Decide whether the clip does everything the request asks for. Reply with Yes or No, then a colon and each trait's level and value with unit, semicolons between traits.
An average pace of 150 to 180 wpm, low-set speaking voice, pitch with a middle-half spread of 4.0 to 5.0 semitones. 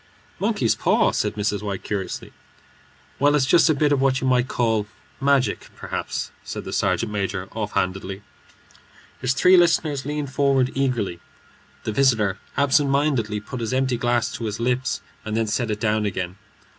Yes: average, 165 wpm; low, 120 Hz; average, 4.6 semitones